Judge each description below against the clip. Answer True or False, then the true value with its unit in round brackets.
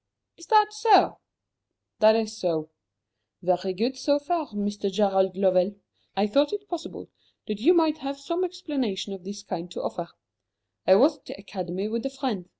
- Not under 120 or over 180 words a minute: True (170 wpm)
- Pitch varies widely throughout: True (7.5 semitones)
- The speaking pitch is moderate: False (215 Hz)